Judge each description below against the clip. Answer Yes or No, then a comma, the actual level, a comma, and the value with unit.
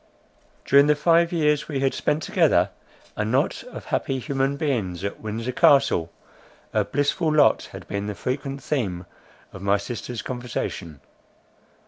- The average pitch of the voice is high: No, low, 135 Hz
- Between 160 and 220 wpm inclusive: No, average, 145 wpm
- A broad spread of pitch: Yes, wide, 5.7 semitones